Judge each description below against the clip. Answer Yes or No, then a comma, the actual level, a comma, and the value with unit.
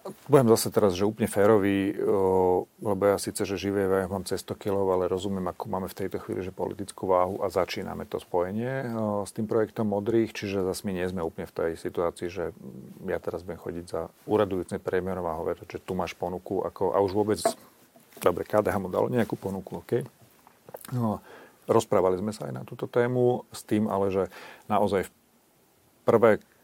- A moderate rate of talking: No, fast, 190 wpm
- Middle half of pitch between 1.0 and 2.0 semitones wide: No, narrow, 2.6 semitones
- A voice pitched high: No, low, 100 Hz